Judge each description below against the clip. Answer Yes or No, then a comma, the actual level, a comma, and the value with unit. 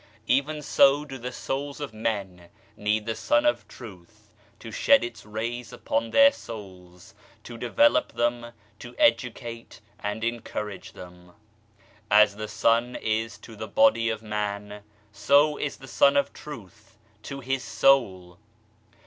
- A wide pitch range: No, average, 4.3 semitones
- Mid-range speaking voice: No, low, 115 Hz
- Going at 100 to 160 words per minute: Yes, average, 150 wpm